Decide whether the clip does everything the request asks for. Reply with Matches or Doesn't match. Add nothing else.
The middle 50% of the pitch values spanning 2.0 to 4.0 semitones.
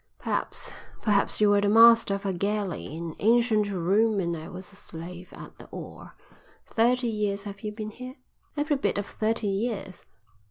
Matches